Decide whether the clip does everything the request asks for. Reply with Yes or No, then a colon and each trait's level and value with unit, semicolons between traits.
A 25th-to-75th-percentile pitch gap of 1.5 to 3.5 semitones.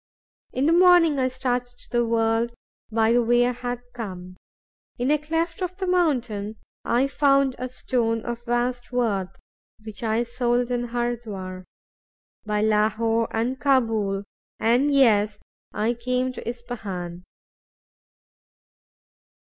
Yes: narrow, 2.5 semitones